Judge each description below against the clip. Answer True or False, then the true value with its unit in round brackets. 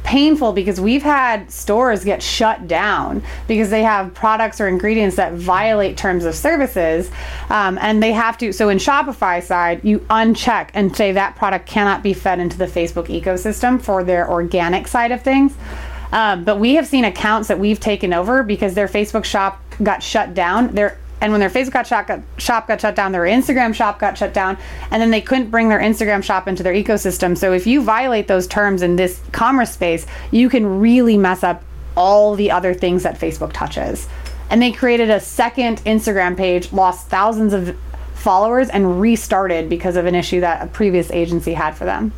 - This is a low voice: False (205 Hz)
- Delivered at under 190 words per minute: False (200 wpm)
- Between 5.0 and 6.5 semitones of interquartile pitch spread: False (3.4 semitones)